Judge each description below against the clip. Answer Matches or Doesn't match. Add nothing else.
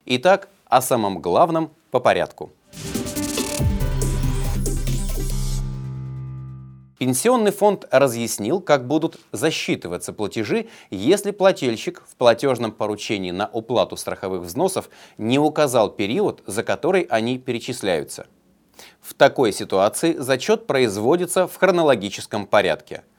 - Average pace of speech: Doesn't match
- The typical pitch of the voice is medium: Doesn't match